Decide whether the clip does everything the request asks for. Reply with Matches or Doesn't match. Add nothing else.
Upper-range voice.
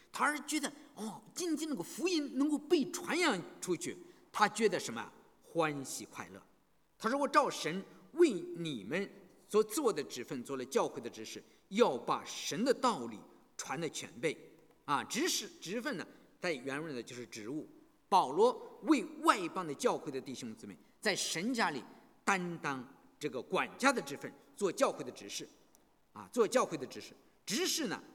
Matches